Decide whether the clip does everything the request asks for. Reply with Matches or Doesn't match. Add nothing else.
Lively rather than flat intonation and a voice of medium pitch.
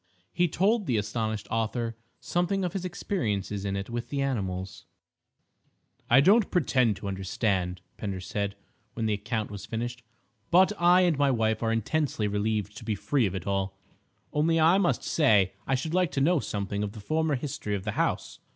Doesn't match